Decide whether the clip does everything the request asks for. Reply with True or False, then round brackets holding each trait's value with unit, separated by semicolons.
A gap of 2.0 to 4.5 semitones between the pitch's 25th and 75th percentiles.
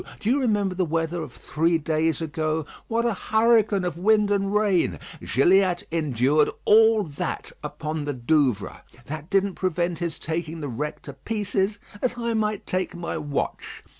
False (5.0 semitones)